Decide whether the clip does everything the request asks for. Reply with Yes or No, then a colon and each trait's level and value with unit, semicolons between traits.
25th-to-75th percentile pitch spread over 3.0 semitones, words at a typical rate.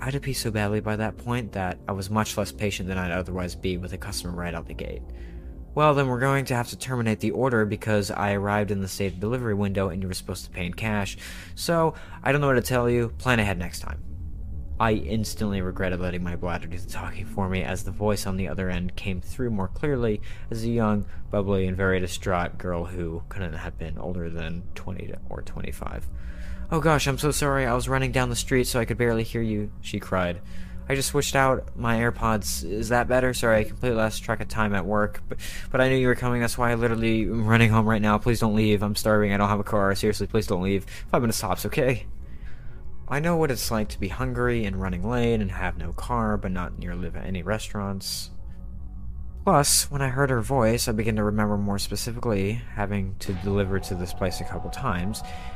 No: average, 4.0 semitones; fast, 230 wpm